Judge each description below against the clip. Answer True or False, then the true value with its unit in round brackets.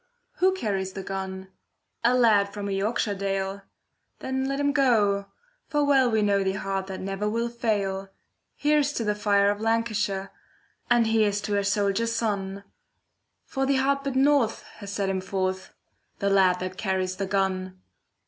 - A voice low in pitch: False (205 Hz)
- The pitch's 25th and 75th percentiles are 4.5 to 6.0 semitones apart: False (3.4 semitones)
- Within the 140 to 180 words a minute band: True (165 wpm)